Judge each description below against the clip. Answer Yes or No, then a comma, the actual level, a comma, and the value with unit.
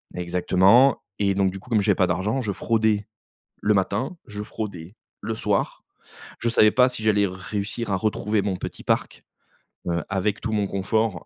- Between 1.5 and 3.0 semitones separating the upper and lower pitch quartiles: Yes, narrow, 2.5 semitones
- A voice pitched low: Yes, low, 105 Hz